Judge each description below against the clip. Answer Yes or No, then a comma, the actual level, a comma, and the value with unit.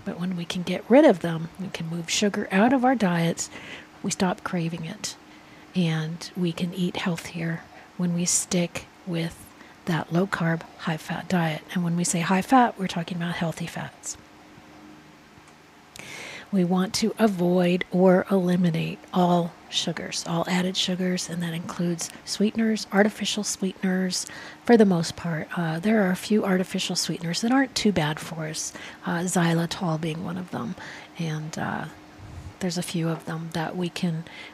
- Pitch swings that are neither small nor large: No, narrow, 2.1 semitones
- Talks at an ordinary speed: Yes, average, 165 wpm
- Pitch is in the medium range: Yes, medium, 180 Hz